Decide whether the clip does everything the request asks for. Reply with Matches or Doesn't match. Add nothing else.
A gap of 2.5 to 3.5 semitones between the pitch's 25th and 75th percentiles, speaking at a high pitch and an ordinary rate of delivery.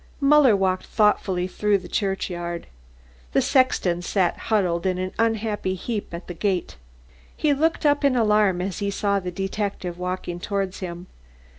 Matches